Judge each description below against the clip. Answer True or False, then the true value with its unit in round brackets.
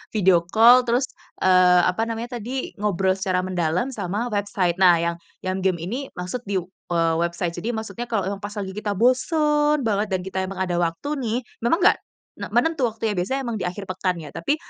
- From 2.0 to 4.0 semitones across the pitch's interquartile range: False (4.5 semitones)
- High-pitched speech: True (200 Hz)